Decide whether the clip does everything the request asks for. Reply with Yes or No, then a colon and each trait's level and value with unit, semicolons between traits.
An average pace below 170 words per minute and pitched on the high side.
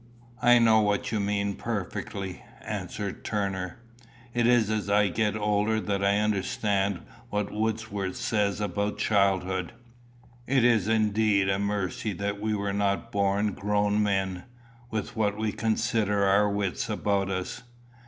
No: average, 140 wpm; low, 105 Hz